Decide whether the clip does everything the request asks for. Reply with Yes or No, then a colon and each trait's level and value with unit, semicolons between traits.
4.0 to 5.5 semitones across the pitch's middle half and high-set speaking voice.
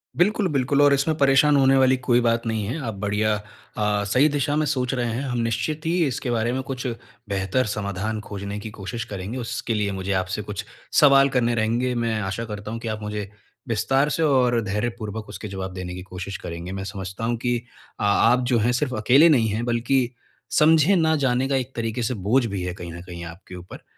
No: average, 4.4 semitones; low, 115 Hz